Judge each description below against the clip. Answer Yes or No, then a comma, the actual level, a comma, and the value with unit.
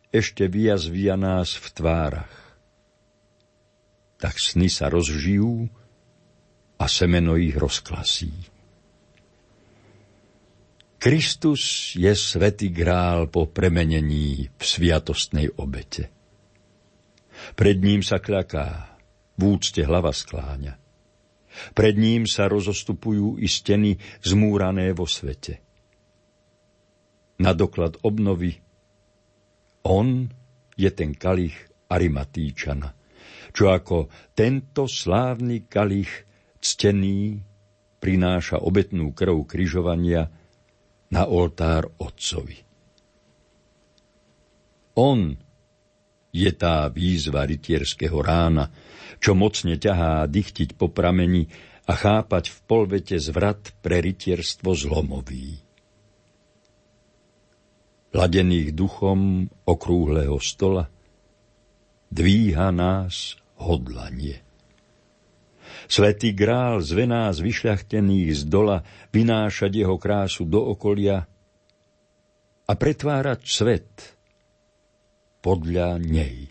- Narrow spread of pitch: No, average, 3.1 semitones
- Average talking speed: No, slow, 80 wpm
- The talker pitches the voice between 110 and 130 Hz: No, very low, 95 Hz